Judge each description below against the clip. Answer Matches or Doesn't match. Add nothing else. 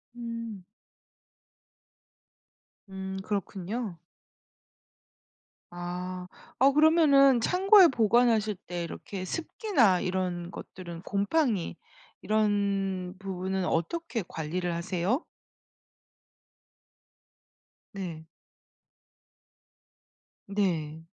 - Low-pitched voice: Doesn't match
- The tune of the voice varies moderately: Matches